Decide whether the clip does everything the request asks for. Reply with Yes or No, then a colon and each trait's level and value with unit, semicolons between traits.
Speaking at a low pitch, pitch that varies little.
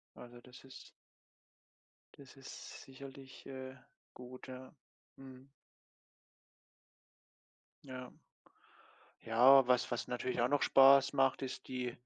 Yes: low, 130 Hz; narrow, 1.2 semitones